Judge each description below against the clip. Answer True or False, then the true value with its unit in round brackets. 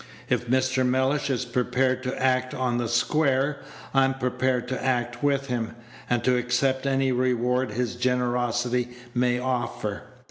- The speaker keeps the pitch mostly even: True (1.3 semitones)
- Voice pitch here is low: True (125 Hz)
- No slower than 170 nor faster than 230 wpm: False (145 wpm)